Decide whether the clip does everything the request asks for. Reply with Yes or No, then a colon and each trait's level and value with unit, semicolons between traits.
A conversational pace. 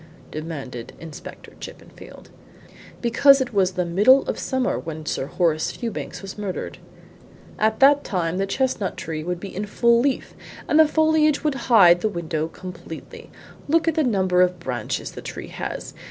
Yes: average, 165 wpm